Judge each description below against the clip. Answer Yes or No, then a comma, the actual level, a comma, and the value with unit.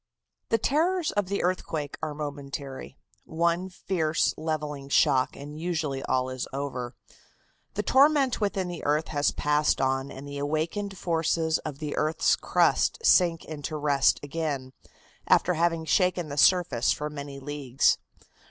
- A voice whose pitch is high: No, medium, 155 Hz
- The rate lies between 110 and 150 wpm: Yes, average, 145 wpm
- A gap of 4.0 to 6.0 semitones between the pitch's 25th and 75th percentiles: No, average, 3.5 semitones